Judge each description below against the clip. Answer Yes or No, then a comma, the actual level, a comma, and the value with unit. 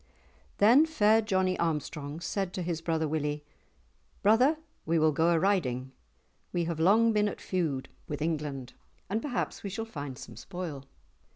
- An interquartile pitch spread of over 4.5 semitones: Yes, wide, 5.4 semitones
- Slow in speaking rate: No, average, 160 wpm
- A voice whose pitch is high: No, medium, 170 Hz